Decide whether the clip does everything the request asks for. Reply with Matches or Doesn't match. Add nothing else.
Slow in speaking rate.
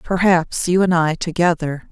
Doesn't match